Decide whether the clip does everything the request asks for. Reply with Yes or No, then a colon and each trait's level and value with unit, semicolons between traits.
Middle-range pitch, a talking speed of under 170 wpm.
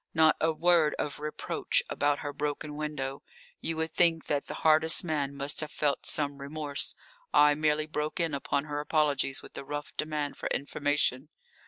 No: medium, 150 Hz; average, 175 wpm